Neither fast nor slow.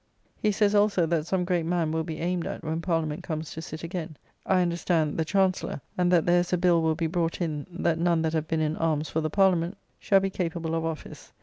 No: fast, 245 wpm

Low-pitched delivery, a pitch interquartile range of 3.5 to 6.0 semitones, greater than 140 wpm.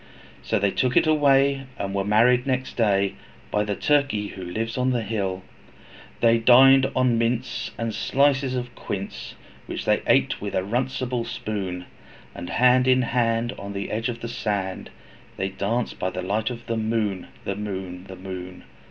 Yes: low, 115 Hz; average, 4.2 semitones; average, 175 wpm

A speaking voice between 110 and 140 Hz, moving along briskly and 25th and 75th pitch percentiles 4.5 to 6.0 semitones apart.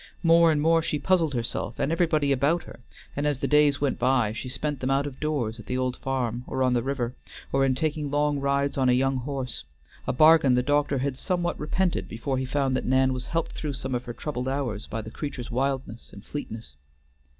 No: low, 135 Hz; fast, 225 wpm; average, 2.8 semitones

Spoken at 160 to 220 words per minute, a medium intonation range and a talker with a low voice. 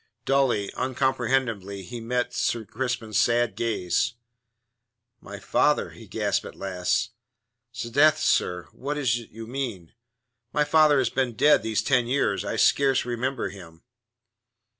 No: slow, 135 wpm; average, 3.4 semitones; low, 120 Hz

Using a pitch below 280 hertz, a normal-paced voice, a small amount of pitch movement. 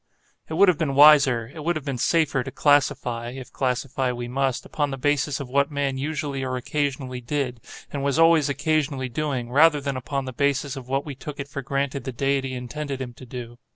No: medium, 140 Hz; fast, 215 wpm; narrow, 2.2 semitones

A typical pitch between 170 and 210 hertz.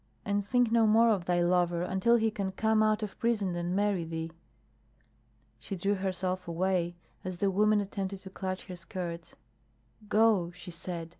Yes: high, 190 Hz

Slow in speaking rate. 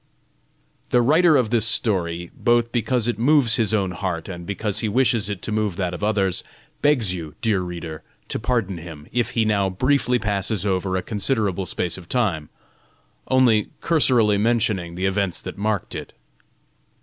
No: average, 170 wpm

